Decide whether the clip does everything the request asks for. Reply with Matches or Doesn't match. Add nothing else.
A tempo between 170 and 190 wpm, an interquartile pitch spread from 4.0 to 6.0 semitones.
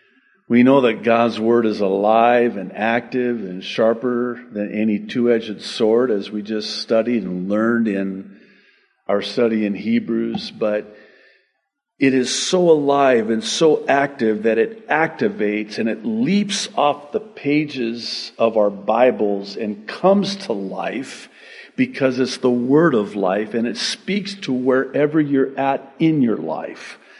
Doesn't match